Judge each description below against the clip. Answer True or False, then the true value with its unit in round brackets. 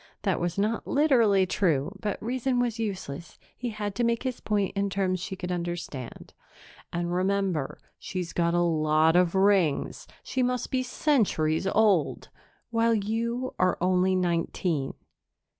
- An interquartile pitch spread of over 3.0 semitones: True (4.7 semitones)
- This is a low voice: False (190 Hz)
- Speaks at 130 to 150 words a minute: True (145 wpm)